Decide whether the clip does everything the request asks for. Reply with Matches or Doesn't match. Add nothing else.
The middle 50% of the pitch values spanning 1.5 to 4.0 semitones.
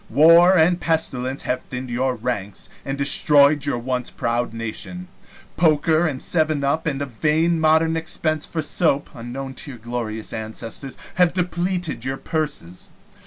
Doesn't match